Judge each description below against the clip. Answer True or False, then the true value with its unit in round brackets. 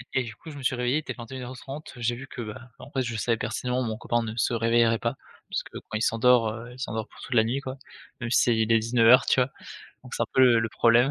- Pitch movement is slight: True (2.1 semitones)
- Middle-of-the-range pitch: False (120 Hz)